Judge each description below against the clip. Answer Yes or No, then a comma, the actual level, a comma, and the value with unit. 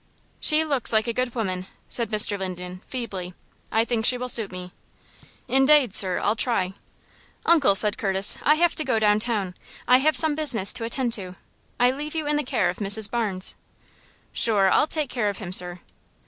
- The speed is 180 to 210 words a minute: Yes, average, 190 wpm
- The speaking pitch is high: Yes, high, 225 Hz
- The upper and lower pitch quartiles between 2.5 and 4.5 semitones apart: No, average, 5.1 semitones